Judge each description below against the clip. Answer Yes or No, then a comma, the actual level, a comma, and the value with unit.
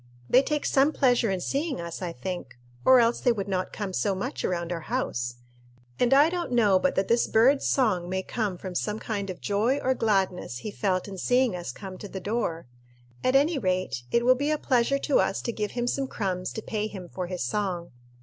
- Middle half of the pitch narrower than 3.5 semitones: No, average, 5.3 semitones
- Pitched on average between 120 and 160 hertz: No, high, 210 Hz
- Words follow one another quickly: Yes, fast, 225 wpm